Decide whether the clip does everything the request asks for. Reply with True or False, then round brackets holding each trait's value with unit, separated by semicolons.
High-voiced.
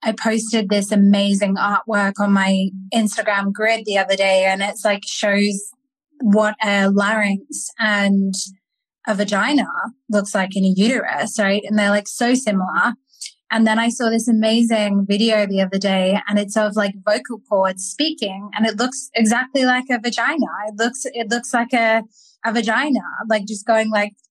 True (215 Hz)